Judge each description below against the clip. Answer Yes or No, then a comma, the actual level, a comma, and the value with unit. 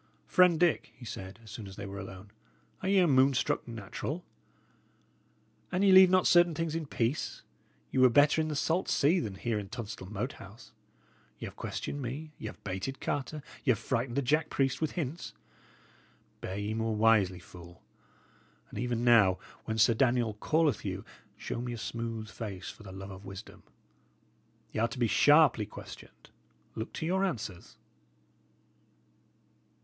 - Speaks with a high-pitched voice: No, low, 120 Hz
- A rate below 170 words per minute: No, average, 175 wpm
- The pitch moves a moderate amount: No, wide, 6.4 semitones